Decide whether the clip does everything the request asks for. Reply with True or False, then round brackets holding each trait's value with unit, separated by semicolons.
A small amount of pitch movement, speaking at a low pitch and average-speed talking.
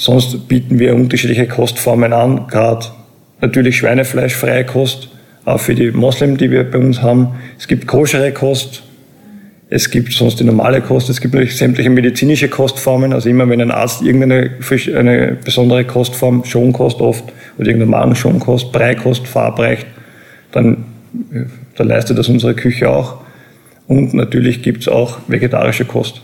True (1.5 semitones; 125 Hz; 150 wpm)